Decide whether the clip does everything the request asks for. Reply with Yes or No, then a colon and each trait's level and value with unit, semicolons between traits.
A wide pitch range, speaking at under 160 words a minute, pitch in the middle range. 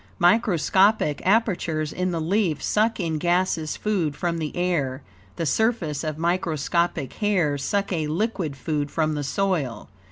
No: average, 4.2 semitones; average, 140 wpm; medium, 170 Hz